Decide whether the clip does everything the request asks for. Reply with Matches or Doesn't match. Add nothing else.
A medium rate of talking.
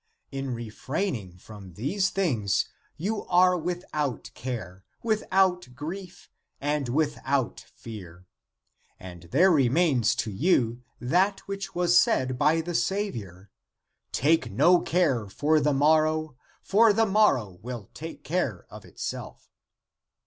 Doesn't match